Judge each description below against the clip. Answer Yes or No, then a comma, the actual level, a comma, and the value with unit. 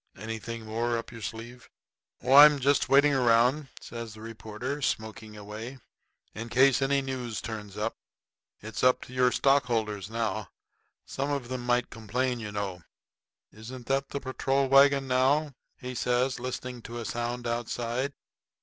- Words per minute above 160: No, average, 150 wpm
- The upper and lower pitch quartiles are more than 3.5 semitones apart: No, average, 3.0 semitones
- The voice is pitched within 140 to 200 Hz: No, low, 120 Hz